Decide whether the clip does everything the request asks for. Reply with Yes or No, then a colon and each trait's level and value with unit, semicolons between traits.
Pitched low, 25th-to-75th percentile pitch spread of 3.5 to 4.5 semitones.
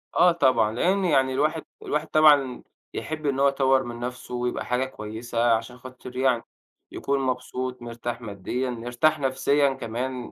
No: low, 130 Hz; narrow, 2.6 semitones